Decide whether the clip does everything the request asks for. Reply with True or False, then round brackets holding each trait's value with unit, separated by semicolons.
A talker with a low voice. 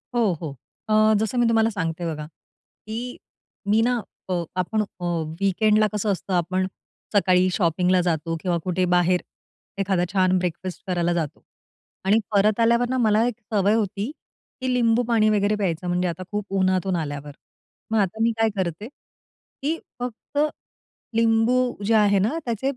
False (200 Hz)